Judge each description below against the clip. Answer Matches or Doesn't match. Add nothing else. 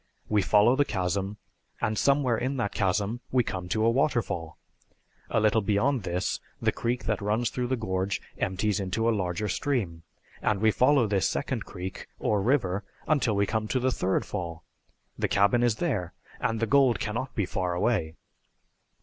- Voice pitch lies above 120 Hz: Doesn't match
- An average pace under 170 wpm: Doesn't match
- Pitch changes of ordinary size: Matches